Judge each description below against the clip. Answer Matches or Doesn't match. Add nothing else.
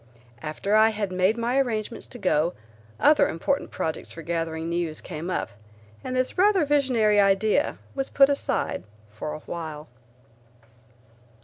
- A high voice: Matches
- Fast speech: Doesn't match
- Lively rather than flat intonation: Matches